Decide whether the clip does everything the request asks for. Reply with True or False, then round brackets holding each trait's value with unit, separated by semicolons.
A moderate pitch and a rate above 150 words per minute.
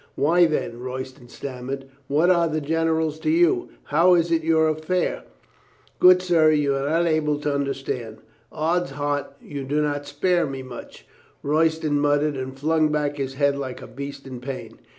True (150 Hz; 170 wpm)